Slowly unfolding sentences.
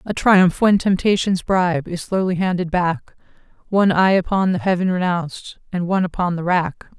No: average, 170 wpm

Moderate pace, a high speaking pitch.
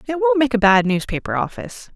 No: fast, 215 wpm; high, 215 Hz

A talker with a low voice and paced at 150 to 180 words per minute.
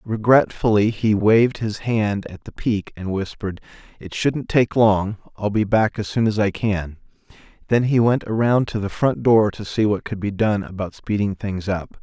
No: low, 105 Hz; average, 195 wpm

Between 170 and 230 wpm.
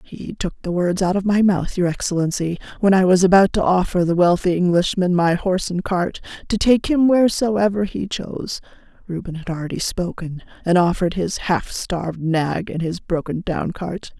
Yes: average, 185 wpm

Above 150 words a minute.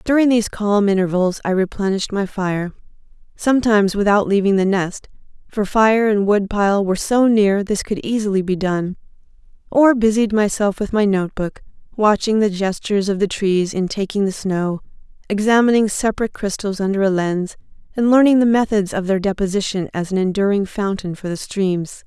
Yes: average, 160 wpm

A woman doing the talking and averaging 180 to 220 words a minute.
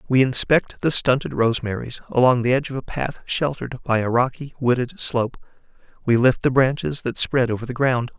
No: male; average, 190 wpm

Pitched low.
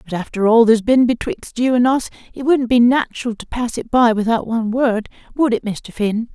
No: high, 235 Hz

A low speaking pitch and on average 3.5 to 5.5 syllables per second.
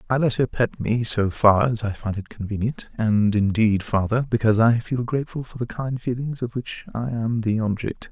Yes: low, 115 Hz; 5.1 syllables/s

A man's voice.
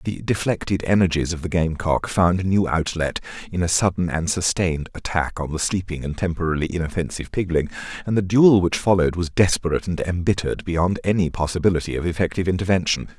Yes: male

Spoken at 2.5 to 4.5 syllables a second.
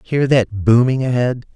Yes: 4.3 syllables/s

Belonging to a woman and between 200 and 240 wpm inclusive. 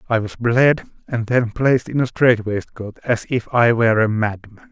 No: male; fast, 205 wpm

